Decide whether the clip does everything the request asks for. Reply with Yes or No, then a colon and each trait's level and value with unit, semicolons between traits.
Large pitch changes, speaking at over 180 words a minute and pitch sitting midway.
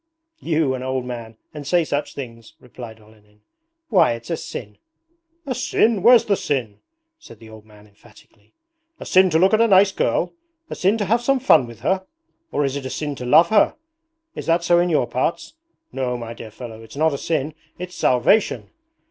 Yes: wide, 7.9 semitones; average, 200 wpm; medium, 145 Hz